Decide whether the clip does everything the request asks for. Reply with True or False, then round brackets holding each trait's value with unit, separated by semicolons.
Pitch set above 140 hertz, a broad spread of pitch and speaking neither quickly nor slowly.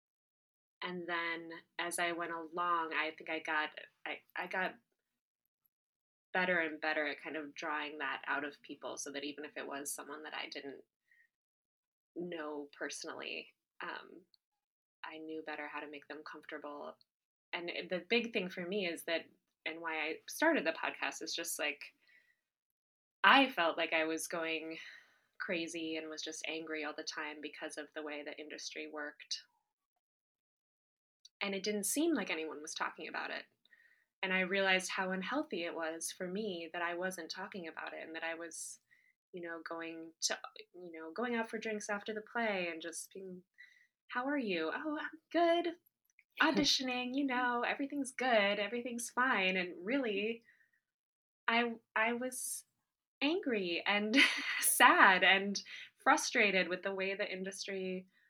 True (185 Hz; 7.0 semitones; 160 wpm)